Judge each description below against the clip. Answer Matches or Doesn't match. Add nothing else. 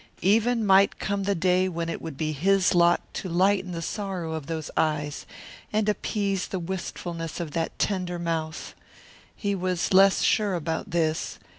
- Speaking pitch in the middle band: Matches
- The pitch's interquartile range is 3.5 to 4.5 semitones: Doesn't match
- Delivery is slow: Doesn't match